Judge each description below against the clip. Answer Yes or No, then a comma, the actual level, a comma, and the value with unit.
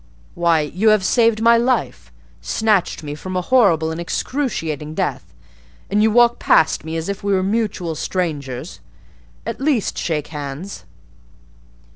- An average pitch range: No, wide, 6.2 semitones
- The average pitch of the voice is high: No, medium, 180 Hz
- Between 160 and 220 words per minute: No, average, 140 wpm